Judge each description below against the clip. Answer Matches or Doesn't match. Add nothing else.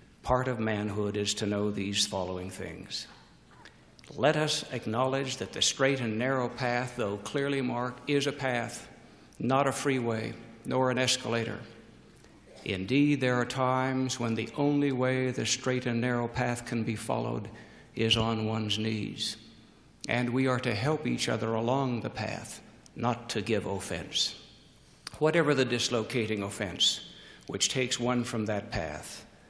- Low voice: Matches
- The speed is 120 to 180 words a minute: Matches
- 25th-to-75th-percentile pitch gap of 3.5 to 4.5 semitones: Doesn't match